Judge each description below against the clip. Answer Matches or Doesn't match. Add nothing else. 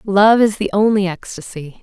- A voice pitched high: Matches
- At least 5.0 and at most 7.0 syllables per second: Doesn't match